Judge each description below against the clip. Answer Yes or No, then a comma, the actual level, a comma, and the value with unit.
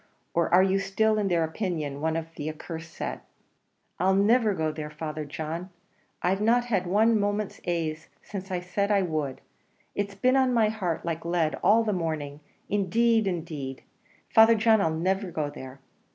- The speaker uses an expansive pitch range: No, average, 4.6 semitones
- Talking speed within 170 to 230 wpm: Yes, average, 175 wpm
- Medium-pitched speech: Yes, medium, 180 Hz